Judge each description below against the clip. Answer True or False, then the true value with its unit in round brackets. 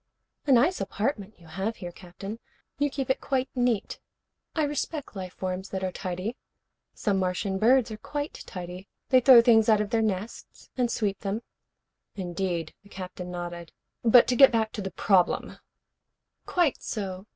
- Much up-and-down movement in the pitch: False (4.8 semitones)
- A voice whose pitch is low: False (210 Hz)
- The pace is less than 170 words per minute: False (175 wpm)